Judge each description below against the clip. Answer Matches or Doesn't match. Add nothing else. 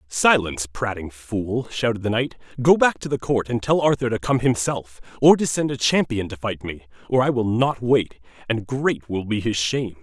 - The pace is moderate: Doesn't match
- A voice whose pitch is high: Doesn't match